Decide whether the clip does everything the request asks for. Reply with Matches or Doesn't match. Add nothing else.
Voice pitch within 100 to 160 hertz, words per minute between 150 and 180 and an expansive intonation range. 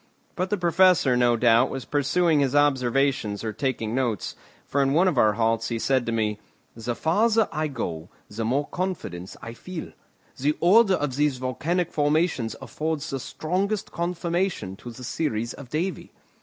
Matches